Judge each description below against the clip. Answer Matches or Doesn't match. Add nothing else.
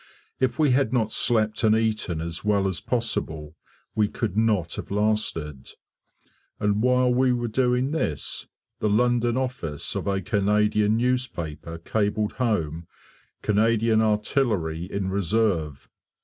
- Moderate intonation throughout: Matches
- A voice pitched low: Matches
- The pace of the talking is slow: Matches